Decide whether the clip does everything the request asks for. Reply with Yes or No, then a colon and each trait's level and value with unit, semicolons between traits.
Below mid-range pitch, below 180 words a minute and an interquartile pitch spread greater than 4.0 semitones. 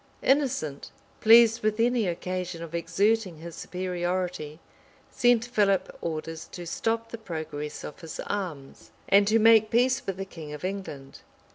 No: medium, 185 Hz; average, 145 wpm; wide, 5.4 semitones